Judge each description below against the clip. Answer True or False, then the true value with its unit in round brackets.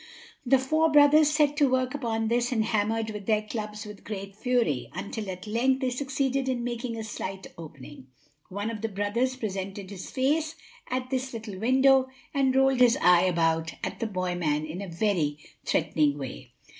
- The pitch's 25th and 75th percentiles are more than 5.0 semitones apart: True (5.4 semitones)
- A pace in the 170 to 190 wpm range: True (180 wpm)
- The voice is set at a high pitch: True (225 Hz)